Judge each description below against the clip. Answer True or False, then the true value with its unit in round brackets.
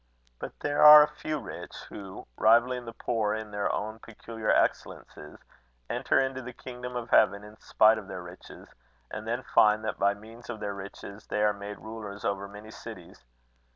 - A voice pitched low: True (110 Hz)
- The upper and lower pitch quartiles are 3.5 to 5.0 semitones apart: False (2.8 semitones)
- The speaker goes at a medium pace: True (185 wpm)